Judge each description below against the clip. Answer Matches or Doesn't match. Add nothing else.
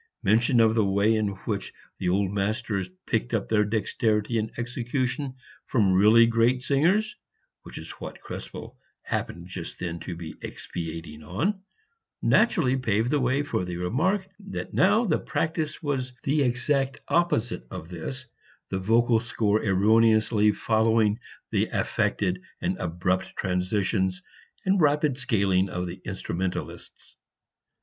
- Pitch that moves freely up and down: Matches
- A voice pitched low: Matches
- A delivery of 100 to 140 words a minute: Matches